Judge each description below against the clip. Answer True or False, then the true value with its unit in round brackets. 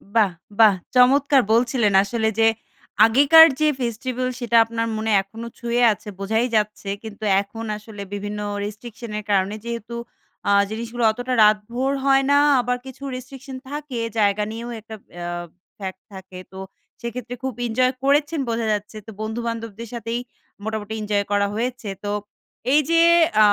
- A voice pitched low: False (230 Hz)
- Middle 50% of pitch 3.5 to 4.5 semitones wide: False (2.8 semitones)